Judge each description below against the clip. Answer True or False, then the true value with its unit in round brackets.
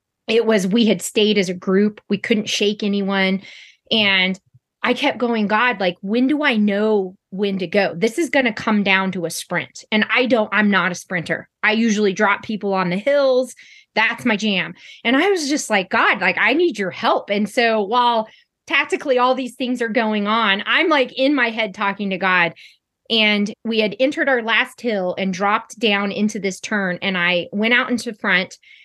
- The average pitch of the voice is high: True (215 Hz)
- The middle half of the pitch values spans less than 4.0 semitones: True (3.6 semitones)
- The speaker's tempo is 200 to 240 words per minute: True (205 wpm)